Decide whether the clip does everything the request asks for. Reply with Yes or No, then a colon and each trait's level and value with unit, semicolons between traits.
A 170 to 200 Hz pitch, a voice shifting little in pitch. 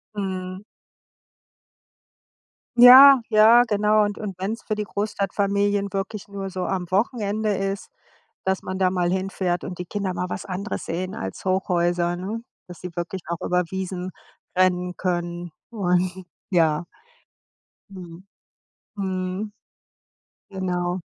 Yes: high, 190 Hz; narrow, 2.2 semitones